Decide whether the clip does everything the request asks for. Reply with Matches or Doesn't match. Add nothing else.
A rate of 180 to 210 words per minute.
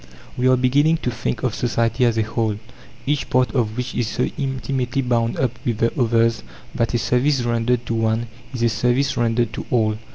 Matches